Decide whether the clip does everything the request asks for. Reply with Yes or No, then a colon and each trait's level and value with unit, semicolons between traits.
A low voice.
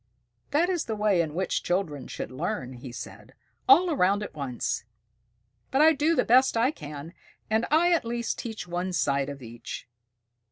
No: high, 190 Hz